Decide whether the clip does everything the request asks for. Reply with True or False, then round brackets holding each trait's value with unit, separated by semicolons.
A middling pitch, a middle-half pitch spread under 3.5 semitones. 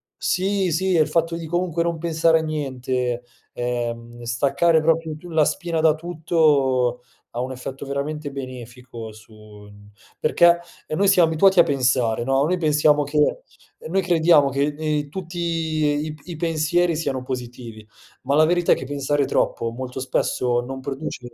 False (150 Hz; 4.5 semitones)